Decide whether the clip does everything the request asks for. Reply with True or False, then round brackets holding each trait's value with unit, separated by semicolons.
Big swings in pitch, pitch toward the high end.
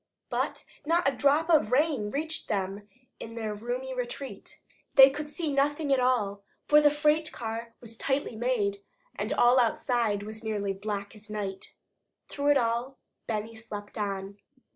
False (5.0 semitones; 235 Hz)